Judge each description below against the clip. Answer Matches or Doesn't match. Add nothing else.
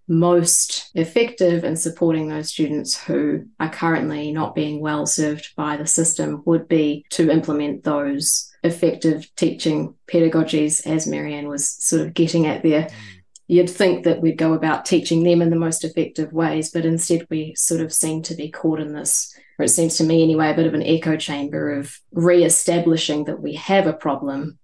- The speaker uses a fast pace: Doesn't match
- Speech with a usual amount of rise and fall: Doesn't match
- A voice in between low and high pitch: Matches